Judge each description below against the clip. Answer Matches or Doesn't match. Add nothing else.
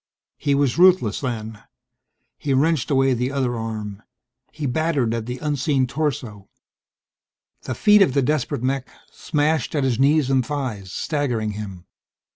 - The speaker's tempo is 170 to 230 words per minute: Doesn't match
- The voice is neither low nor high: Doesn't match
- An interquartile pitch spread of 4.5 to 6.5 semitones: Doesn't match